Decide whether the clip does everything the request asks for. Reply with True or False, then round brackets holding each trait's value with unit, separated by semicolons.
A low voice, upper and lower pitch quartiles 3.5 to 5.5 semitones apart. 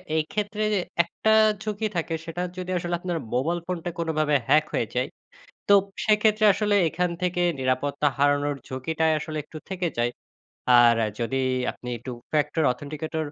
False (160 Hz; 3.9 semitones)